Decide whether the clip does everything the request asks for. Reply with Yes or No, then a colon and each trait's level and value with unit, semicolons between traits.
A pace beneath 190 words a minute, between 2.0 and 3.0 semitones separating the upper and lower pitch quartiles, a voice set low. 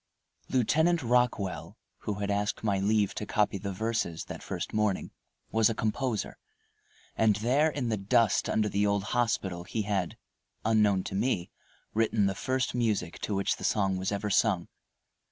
Yes: average, 165 wpm; average, 2.7 semitones; low, 105 Hz